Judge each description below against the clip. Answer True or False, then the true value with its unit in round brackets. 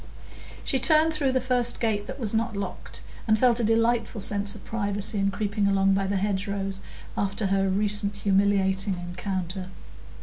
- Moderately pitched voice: False (200 Hz)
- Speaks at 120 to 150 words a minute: False (165 wpm)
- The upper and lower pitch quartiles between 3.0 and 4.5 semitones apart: False (2.6 semitones)